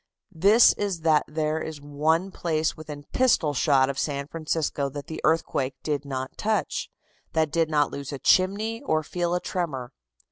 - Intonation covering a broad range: No, average, 3.1 semitones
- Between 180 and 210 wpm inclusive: No, average, 170 wpm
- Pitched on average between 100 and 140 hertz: No, medium, 155 Hz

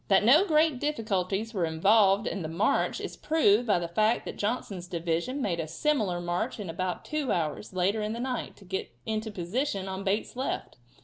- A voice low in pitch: No, high, 205 Hz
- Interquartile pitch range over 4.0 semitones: Yes, average, 5.2 semitones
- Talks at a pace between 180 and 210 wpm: Yes, average, 195 wpm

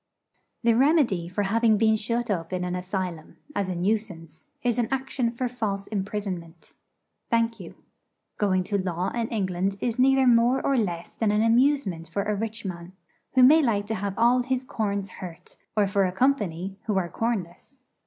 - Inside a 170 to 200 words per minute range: Yes, average, 180 wpm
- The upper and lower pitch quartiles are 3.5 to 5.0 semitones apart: Yes, average, 4.1 semitones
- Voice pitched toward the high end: Yes, high, 210 Hz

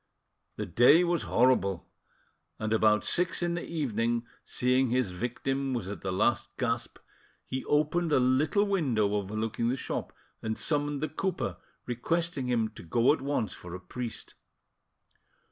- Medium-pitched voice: No, low, 125 Hz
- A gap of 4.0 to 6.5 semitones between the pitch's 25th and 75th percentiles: Yes, average, 5.0 semitones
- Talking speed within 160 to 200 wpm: No, average, 150 wpm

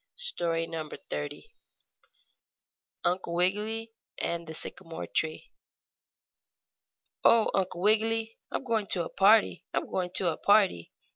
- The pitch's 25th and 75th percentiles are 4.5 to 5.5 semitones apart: Yes, average, 4.8 semitones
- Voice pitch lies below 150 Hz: No, high, 190 Hz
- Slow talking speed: Yes, slow, 115 wpm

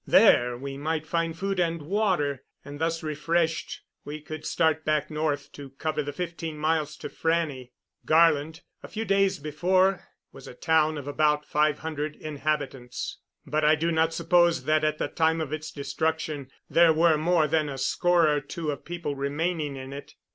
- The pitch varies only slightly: Yes, narrow, 2.1 semitones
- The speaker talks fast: No, average, 175 wpm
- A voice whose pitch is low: No, medium, 155 Hz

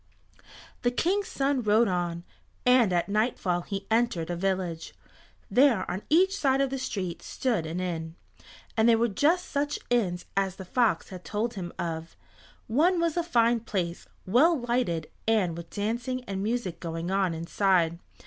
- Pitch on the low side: No, high, 210 Hz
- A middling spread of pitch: No, wide, 6.0 semitones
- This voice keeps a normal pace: Yes, average, 165 wpm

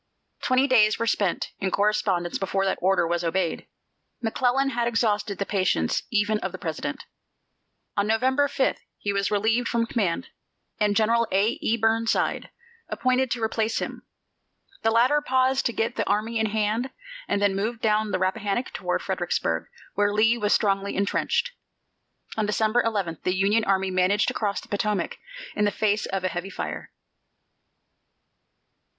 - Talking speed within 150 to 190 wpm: Yes, average, 160 wpm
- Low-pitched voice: No, high, 210 Hz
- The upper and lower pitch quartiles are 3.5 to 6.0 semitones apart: No, average, 2.7 semitones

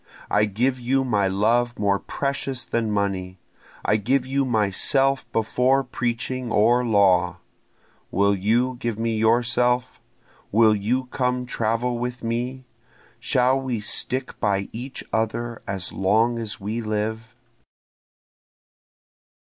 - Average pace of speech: No, slow, 120 wpm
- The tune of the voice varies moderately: Yes, average, 3.1 semitones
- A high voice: No, low, 115 Hz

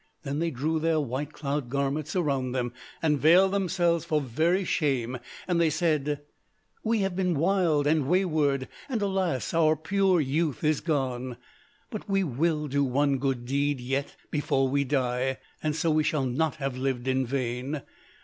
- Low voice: No, medium, 145 Hz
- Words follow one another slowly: No, average, 170 wpm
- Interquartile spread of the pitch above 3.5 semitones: Yes, average, 3.9 semitones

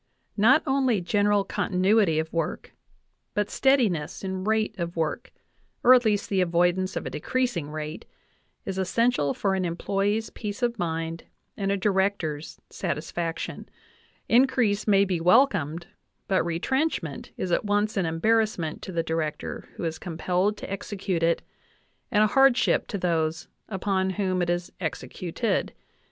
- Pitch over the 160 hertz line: Yes, high, 190 Hz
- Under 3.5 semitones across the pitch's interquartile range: No, average, 4.0 semitones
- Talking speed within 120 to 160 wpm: Yes, average, 155 wpm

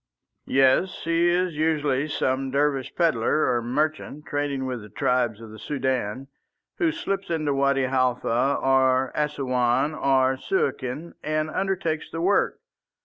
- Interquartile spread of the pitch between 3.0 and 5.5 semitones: Yes, average, 3.3 semitones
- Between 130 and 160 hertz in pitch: Yes, medium, 140 Hz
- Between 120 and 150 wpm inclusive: Yes, slow, 135 wpm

